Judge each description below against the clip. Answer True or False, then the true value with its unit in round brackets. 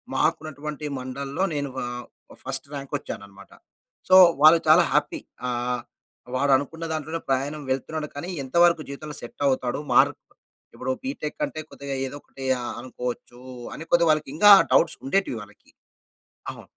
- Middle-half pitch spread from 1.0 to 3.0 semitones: False (3.4 semitones)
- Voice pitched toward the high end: False (140 Hz)